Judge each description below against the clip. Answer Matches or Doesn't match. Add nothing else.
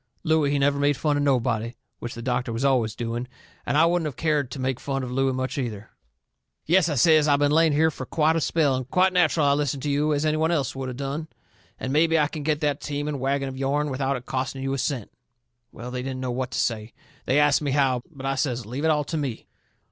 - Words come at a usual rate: Doesn't match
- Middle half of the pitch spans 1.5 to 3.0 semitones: Matches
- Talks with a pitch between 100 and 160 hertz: Matches